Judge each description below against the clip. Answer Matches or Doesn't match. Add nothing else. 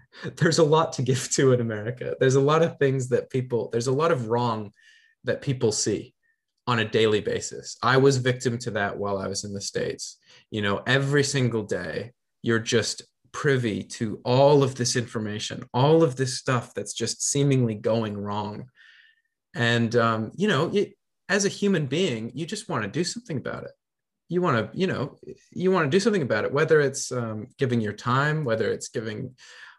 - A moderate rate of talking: Matches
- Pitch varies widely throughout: Matches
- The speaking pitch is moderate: Doesn't match